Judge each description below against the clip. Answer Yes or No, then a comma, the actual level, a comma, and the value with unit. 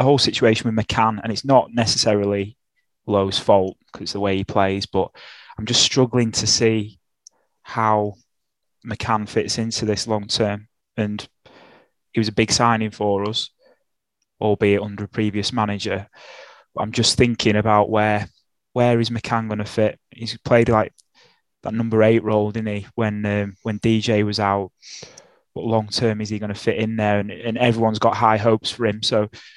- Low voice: Yes, low, 110 Hz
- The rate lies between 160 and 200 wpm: Yes, average, 175 wpm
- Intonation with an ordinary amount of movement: No, narrow, 1.8 semitones